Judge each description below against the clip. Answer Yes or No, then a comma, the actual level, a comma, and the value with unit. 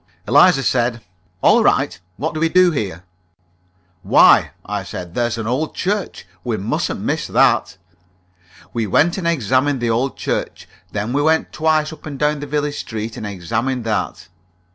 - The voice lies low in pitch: Yes, low, 130 Hz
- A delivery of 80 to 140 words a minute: No, average, 165 wpm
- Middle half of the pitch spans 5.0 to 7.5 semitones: Yes, wide, 5.6 semitones